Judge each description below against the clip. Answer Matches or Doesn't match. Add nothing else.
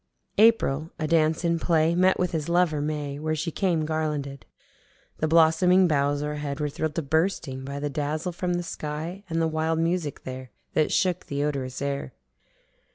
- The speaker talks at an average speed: Matches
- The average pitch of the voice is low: Doesn't match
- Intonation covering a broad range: Doesn't match